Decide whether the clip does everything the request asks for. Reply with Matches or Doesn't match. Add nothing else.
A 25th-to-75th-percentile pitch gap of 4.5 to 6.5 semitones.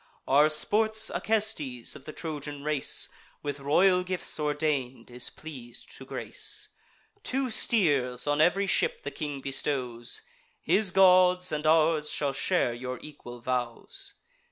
Matches